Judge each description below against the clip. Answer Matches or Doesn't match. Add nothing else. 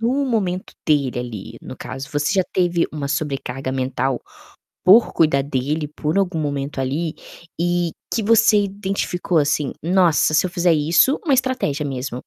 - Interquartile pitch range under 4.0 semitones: Doesn't match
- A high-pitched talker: Doesn't match